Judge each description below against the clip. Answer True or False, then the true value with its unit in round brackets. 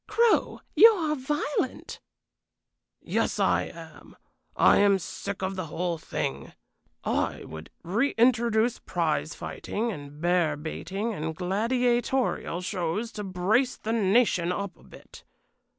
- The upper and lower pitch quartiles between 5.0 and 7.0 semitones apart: True (5.3 semitones)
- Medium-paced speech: False (120 wpm)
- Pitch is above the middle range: True (200 Hz)